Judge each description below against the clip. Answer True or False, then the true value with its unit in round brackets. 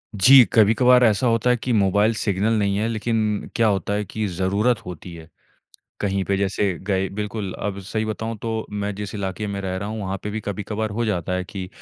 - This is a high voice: False (105 Hz)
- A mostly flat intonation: True (2.3 semitones)